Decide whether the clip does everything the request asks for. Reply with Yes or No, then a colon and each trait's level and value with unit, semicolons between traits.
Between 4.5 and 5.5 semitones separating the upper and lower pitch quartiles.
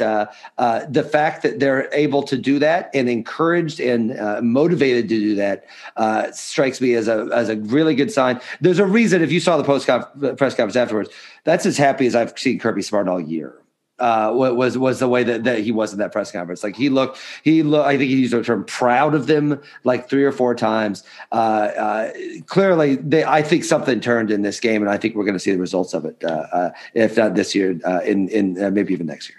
Yes: average, 5.2 semitones